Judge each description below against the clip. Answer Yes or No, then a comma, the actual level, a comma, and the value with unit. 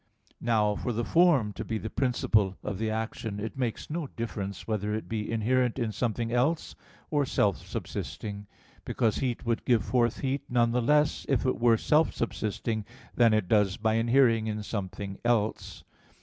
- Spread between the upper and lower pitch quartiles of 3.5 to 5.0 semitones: No, narrow, 2.6 semitones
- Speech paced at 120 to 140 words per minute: No, average, 175 wpm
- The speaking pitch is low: Yes, low, 115 Hz